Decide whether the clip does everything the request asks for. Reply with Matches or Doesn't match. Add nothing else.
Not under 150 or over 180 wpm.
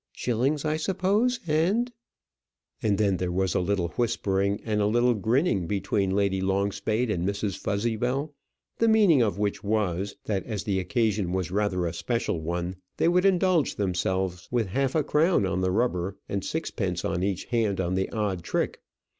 Matches